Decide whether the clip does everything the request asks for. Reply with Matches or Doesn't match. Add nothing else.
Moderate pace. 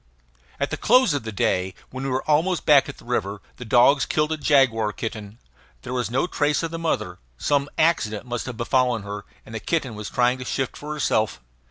Doesn't match